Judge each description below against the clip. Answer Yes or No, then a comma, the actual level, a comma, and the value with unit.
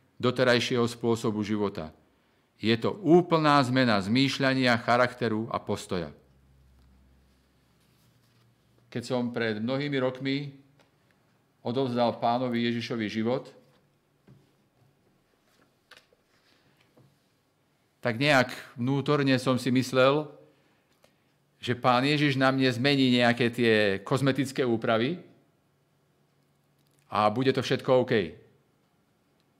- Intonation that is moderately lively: Yes, average, 3.0 semitones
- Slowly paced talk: Yes, slow, 85 wpm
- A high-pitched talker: No, low, 125 Hz